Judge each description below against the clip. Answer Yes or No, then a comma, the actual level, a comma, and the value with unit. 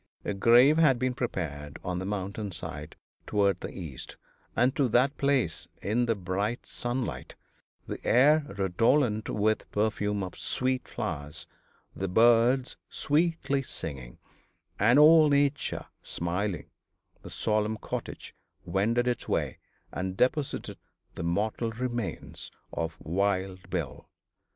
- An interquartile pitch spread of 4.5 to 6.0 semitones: Yes, average, 5.3 semitones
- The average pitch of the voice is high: No, low, 110 Hz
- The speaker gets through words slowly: Yes, slow, 125 wpm